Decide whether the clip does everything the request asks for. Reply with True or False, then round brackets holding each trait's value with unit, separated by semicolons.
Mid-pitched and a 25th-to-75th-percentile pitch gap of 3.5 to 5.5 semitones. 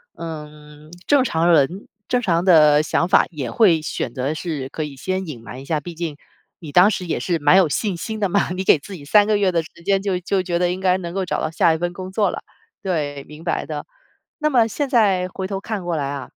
True (175 Hz; 4.1 semitones)